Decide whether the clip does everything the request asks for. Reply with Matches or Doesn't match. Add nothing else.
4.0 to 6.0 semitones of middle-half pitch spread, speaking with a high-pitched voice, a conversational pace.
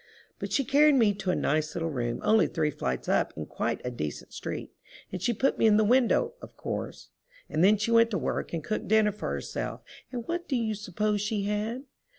Doesn't match